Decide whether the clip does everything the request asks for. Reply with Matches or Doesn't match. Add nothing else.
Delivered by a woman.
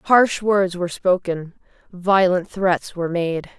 Matches